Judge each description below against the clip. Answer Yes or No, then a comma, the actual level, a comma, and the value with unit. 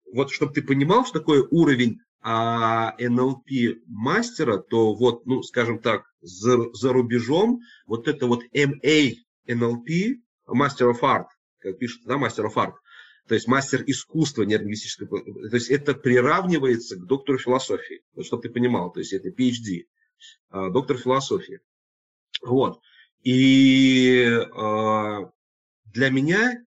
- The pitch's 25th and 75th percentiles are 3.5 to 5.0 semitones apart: Yes, average, 3.9 semitones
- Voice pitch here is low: Yes, low, 125 Hz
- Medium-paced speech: Yes, average, 135 wpm